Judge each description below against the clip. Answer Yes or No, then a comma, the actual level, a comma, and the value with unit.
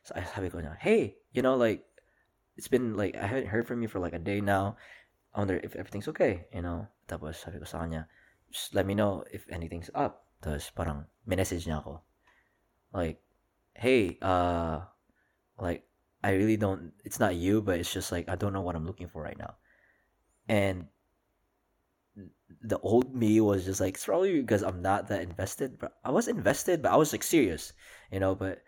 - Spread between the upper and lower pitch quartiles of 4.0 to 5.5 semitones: No, average, 3.1 semitones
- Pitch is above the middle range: No, very low, 95 Hz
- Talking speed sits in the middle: No, fast, 175 wpm